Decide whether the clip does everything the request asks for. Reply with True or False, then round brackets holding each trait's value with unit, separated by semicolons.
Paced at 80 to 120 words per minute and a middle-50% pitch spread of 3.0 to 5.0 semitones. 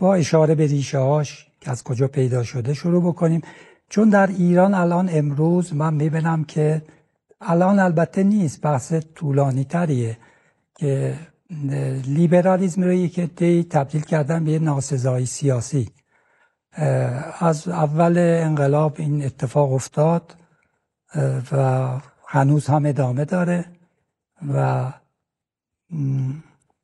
True (105 wpm; 3.7 semitones)